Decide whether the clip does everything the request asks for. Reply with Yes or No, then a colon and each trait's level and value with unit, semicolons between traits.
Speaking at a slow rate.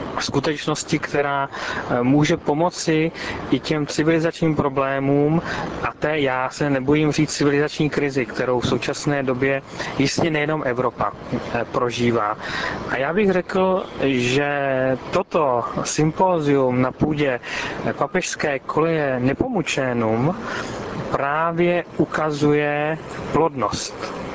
Yes: slow, 95 wpm